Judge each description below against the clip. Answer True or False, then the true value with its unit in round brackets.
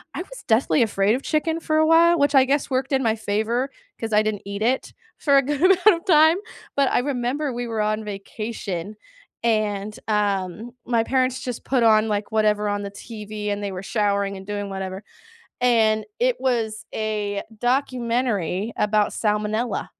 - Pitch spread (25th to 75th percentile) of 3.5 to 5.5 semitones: True (3.9 semitones)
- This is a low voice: False (220 Hz)